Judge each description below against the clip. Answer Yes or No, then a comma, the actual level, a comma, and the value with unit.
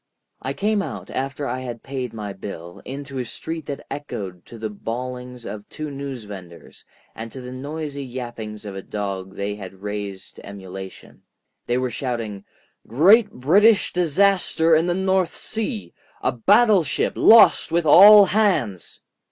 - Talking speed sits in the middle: Yes, average, 150 wpm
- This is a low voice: Yes, low, 125 Hz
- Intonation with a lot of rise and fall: Yes, wide, 7.7 semitones